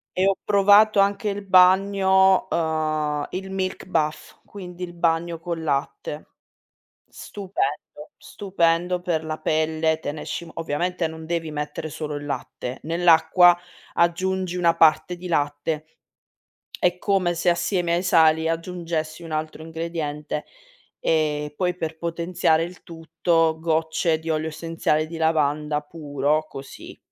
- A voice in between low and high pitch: Yes, medium, 165 Hz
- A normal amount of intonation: No, narrow, 2.3 semitones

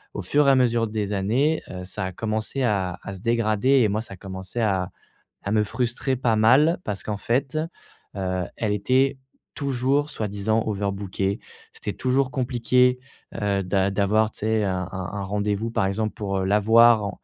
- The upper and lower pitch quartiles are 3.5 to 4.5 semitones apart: Yes, average, 3.8 semitones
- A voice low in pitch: Yes, low, 110 Hz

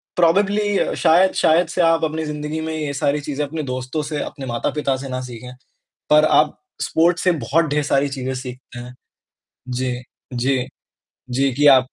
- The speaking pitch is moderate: Yes, medium, 145 Hz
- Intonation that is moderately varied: Yes, average, 3.6 semitones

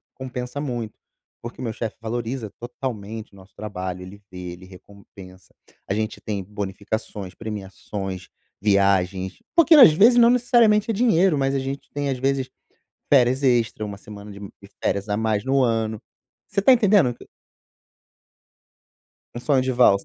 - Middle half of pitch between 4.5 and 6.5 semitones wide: Yes, average, 5.3 semitones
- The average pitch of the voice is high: No, low, 115 Hz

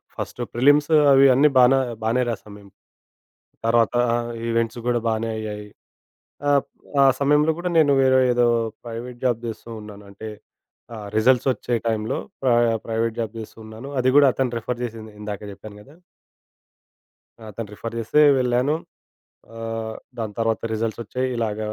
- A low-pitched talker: Yes, low, 115 Hz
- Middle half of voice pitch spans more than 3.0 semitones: No, average, 2.7 semitones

